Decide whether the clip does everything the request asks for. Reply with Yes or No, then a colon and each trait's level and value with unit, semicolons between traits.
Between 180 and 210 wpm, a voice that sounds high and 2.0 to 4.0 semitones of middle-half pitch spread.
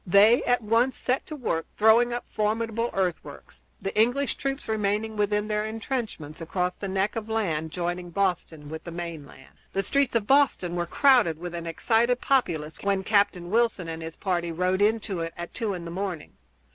No: average, 185 wpm; high, 200 Hz; average, 4.6 semitones